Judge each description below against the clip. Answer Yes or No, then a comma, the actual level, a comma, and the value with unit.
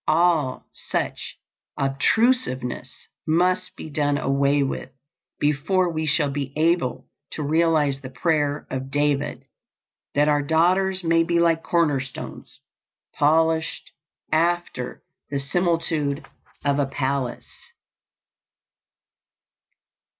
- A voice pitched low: No, medium, 150 Hz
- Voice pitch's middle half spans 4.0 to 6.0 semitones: No, average, 3.1 semitones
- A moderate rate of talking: No, slow, 100 wpm